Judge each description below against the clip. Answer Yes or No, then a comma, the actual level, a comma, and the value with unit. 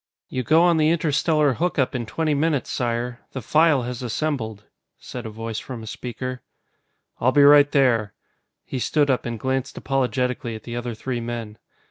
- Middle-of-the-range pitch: No, low, 130 Hz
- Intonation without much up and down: No, average, 3.6 semitones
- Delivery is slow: No, average, 175 wpm